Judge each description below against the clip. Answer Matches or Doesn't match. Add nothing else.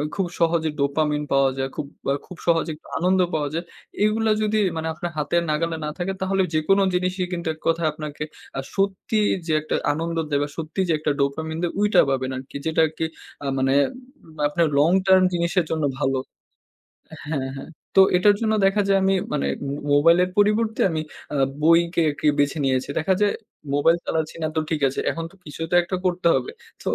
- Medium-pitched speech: Matches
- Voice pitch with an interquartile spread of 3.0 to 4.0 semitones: Matches